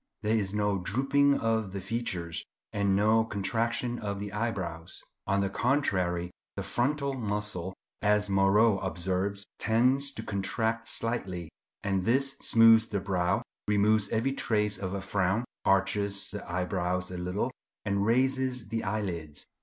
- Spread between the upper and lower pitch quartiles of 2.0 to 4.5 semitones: Yes, average, 3.0 semitones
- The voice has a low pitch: Yes, low, 105 Hz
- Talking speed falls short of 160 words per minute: Yes, average, 140 wpm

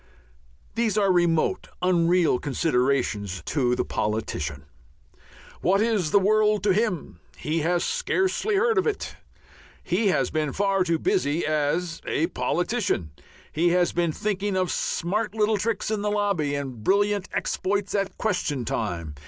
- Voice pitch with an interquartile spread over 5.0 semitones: Yes, wide, 5.6 semitones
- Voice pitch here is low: No, medium, 180 Hz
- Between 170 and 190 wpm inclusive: No, average, 145 wpm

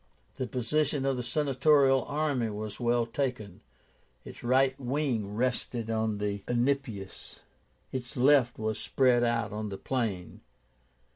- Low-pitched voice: Yes, low, 120 Hz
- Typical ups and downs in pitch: Yes, average, 3.5 semitones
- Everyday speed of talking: No, slow, 130 wpm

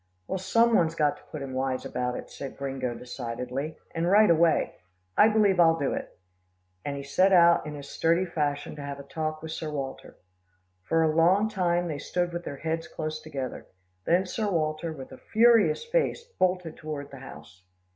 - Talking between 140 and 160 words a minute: No, average, 195 wpm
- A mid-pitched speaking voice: Yes, medium, 160 Hz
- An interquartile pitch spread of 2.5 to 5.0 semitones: Yes, average, 4.0 semitones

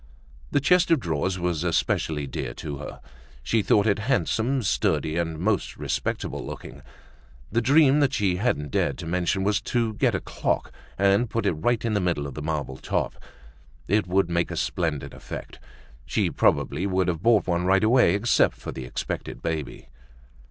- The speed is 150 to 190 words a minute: Yes, average, 180 wpm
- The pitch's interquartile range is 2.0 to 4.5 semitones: No, wide, 5.6 semitones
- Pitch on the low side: Yes, very low, 95 Hz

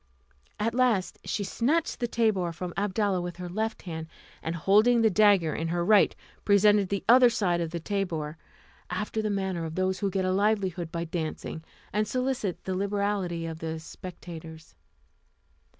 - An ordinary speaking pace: Yes, average, 165 wpm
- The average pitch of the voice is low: No, high, 190 Hz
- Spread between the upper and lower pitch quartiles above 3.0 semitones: Yes, average, 3.6 semitones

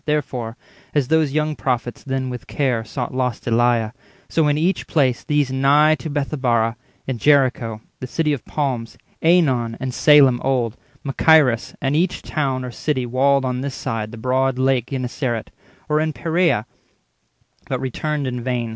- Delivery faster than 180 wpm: No, average, 155 wpm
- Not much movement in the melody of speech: No, average, 3.4 semitones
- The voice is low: Yes, low, 130 Hz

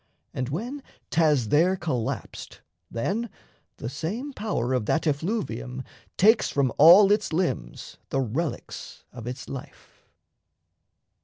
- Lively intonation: Yes, wide, 7.8 semitones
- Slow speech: Yes, slow, 120 wpm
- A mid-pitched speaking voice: Yes, medium, 155 Hz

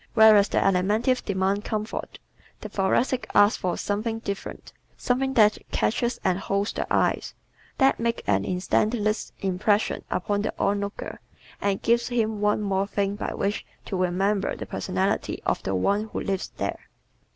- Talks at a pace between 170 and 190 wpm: No, average, 150 wpm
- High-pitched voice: Yes, high, 205 Hz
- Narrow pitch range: Yes, narrow, 2.1 semitones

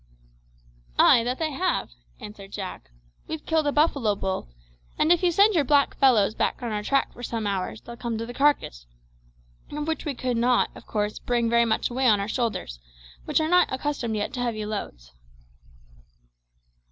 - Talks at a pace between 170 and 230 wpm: Yes, average, 185 wpm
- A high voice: Yes, high, 240 Hz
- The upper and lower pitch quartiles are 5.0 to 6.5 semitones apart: Yes, wide, 5.5 semitones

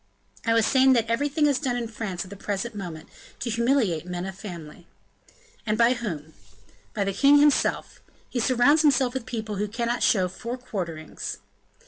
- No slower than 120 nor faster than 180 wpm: Yes, average, 175 wpm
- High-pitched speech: Yes, high, 230 Hz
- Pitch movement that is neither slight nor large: Yes, average, 4.9 semitones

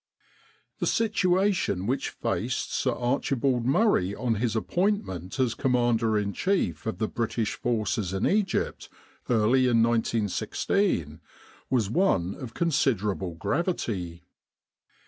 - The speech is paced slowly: Yes, slow, 110 wpm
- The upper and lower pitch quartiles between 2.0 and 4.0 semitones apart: No, average, 4.9 semitones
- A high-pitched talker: No, low, 115 Hz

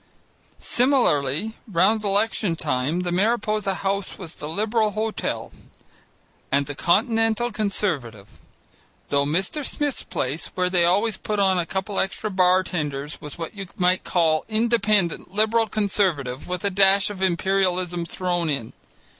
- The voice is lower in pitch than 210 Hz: Yes, high, 190 Hz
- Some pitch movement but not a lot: Yes, average, 4.1 semitones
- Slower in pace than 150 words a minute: Yes, average, 140 wpm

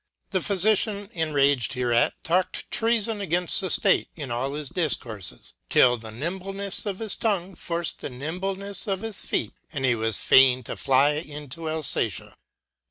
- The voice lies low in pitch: No, medium, 160 Hz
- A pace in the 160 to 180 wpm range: No, average, 150 wpm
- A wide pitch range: Yes, wide, 6.9 semitones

